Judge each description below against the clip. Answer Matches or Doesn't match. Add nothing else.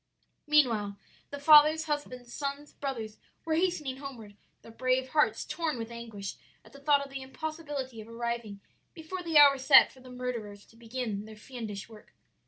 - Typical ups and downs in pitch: Matches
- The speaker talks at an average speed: Matches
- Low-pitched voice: Doesn't match